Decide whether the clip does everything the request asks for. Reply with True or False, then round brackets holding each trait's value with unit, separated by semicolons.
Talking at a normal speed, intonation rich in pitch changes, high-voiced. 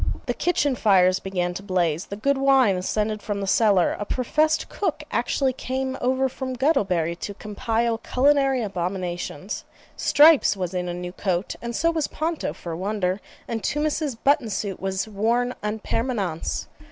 True (165 wpm; 6.0 semitones; 215 Hz)